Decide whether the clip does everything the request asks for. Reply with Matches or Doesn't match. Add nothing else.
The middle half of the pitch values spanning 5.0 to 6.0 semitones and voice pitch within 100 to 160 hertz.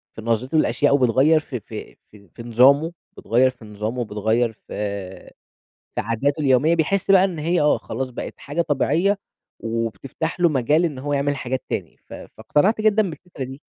Matches